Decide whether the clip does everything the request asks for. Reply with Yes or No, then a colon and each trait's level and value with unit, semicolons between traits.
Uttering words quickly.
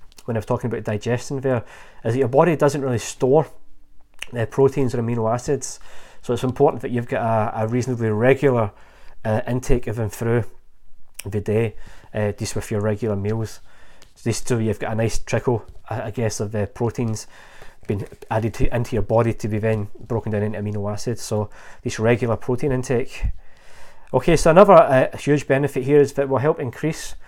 No: average, 195 wpm